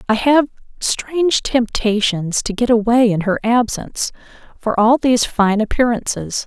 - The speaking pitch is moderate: No, high, 230 Hz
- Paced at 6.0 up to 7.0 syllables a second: No, 4.5 syllables/s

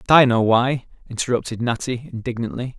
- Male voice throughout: Yes, male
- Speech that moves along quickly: No, average, 150 wpm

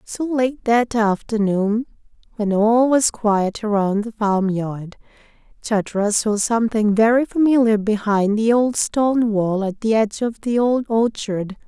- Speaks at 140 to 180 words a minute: Yes, average, 145 wpm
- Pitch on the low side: No, high, 220 Hz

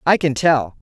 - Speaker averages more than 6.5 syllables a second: No, 4.4 syllables/s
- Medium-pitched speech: Yes, medium, 155 Hz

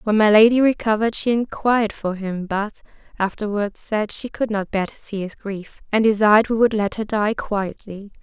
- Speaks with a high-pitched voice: Yes, high, 210 Hz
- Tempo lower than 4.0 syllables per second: No, 5.1 syllables/s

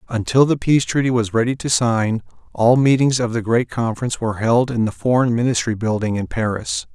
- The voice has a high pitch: No, low, 120 Hz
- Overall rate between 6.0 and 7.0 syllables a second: No, 5.8 syllables/s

